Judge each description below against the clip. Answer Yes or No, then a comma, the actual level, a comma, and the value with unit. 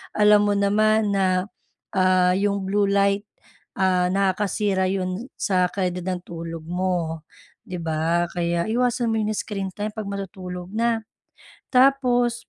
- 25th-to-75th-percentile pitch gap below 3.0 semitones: Yes, narrow, 2.5 semitones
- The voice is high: Yes, high, 195 Hz